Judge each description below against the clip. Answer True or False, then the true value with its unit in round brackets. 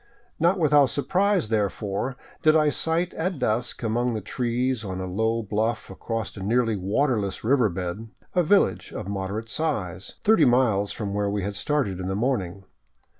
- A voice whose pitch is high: False (115 Hz)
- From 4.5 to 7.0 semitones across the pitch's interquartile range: True (5.5 semitones)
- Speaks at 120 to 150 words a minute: False (170 wpm)